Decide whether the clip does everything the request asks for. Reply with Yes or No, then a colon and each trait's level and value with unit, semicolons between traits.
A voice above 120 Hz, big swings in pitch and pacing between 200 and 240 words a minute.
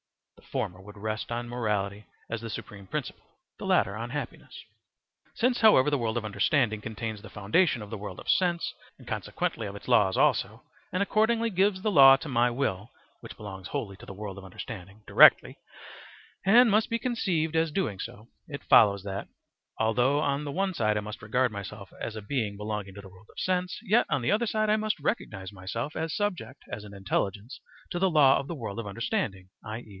No: low, 115 Hz; wide, 8.2 semitones; fast, 205 wpm